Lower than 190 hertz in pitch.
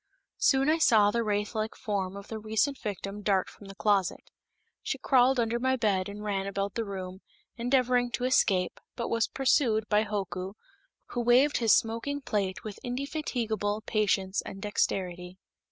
No: high, 215 Hz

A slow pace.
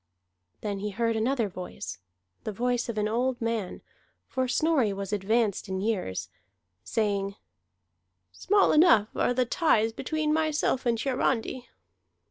Yes: slow, 130 wpm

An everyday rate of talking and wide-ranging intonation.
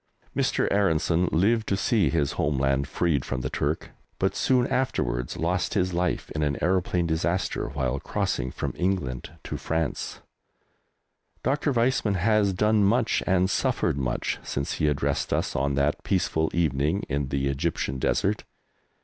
Yes: average, 150 wpm; wide, 5.7 semitones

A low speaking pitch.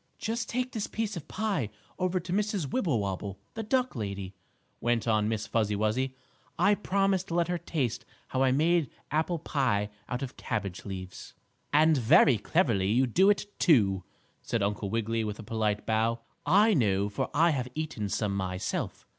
Yes: low, 130 Hz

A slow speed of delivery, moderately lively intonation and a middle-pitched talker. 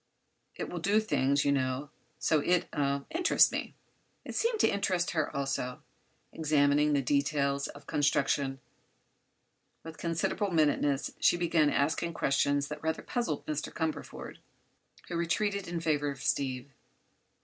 Yes: slow, 130 wpm; average, 3.2 semitones; medium, 150 Hz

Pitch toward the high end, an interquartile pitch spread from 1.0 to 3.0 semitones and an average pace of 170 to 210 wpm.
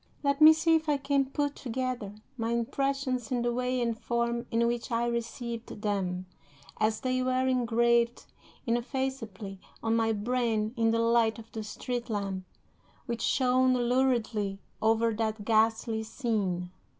No: high, 235 Hz; narrow, 2.4 semitones; average, 150 wpm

